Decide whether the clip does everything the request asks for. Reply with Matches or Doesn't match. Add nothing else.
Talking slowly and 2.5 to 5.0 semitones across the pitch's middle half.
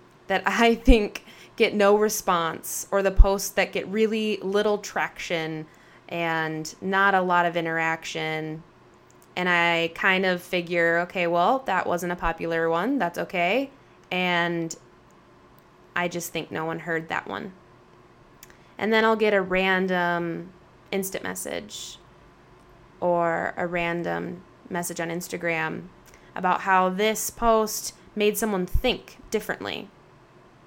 Matches